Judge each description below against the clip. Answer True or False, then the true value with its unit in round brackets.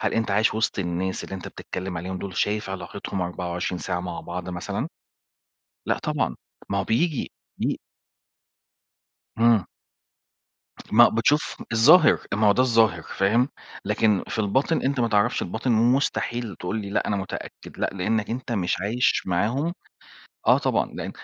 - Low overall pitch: True (105 Hz)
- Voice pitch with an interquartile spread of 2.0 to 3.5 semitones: False (3.9 semitones)